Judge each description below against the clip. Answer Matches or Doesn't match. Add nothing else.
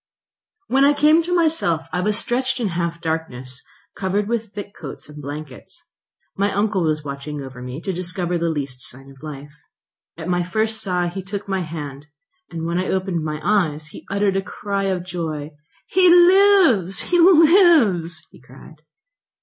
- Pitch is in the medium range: Matches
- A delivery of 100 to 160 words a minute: Doesn't match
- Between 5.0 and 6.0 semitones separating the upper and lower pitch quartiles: Matches